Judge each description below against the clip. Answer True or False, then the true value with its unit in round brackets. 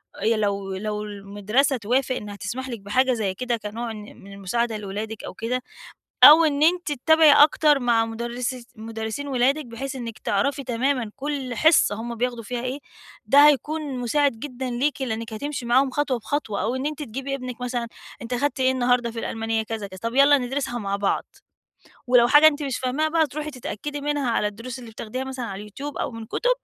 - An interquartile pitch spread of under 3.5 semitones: False (3.8 semitones)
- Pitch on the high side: True (245 Hz)